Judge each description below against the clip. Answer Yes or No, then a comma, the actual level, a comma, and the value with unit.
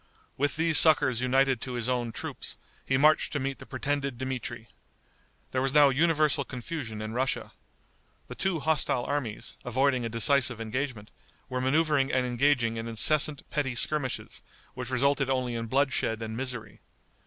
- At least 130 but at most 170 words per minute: Yes, average, 155 wpm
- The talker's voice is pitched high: No, low, 130 Hz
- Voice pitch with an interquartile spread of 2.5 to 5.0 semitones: Yes, average, 3.1 semitones